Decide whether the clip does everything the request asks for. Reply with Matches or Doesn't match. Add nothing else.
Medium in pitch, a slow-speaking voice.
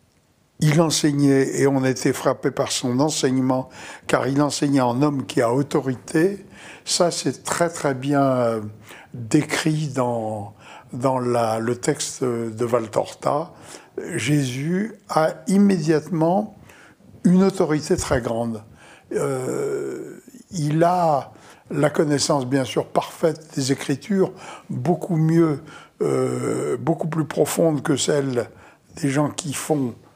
Matches